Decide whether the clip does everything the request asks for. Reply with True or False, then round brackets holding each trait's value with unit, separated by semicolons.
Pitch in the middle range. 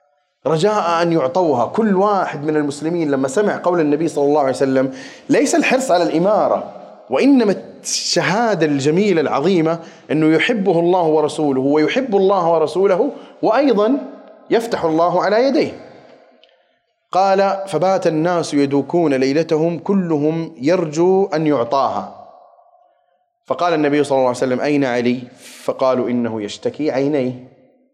True (165 Hz)